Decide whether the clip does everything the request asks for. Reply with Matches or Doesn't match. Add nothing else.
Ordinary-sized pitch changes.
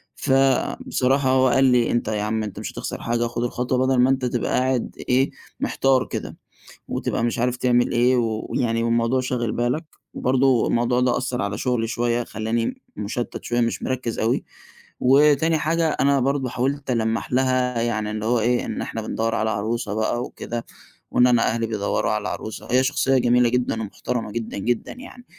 Doesn't match